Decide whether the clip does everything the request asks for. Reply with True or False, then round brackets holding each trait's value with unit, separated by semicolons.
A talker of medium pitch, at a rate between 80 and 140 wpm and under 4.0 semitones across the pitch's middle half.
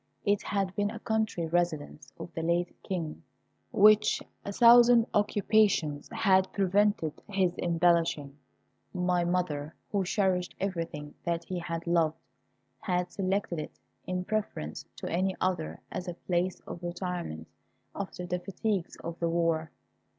True (180 Hz; 135 wpm; 2.8 semitones)